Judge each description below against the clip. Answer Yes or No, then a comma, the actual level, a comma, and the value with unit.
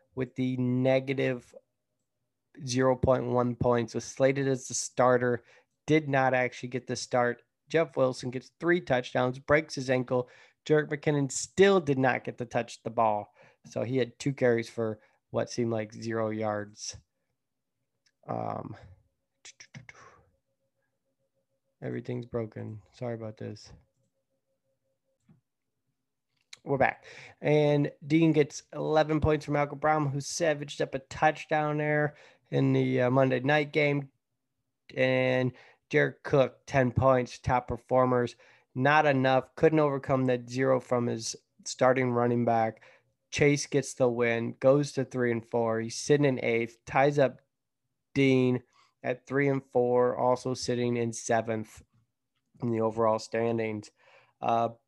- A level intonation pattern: Yes, narrow, 2.1 semitones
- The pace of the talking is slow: Yes, slow, 130 wpm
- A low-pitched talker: Yes, low, 130 Hz